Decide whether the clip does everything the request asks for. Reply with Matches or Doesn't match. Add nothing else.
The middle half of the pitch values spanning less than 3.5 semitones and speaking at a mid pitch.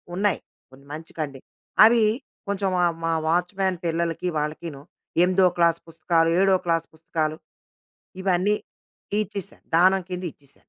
Matches